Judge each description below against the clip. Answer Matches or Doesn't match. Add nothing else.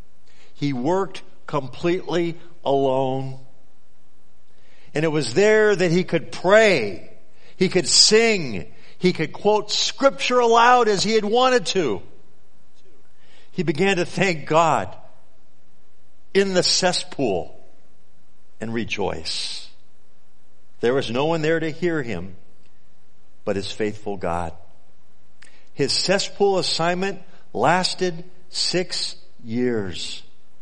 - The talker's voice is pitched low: Doesn't match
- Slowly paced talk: Matches